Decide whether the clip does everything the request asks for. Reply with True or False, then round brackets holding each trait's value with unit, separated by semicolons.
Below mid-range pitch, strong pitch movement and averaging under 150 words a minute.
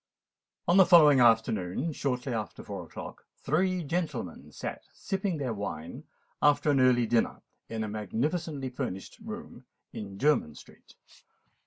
True (130 Hz; 5.9 semitones; 135 wpm)